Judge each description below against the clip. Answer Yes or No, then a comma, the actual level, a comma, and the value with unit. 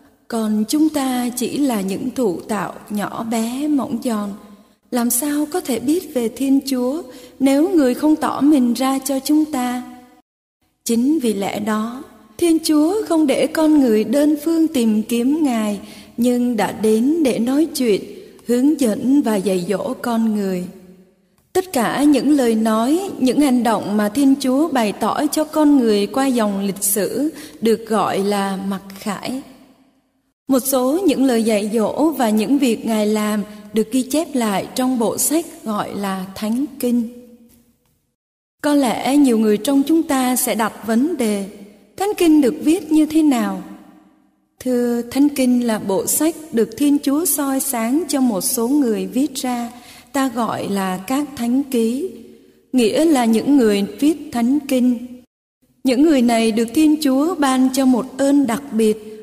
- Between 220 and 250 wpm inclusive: No, slow, 165 wpm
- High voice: Yes, very high, 250 Hz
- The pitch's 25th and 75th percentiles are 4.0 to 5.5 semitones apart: Yes, average, 4.3 semitones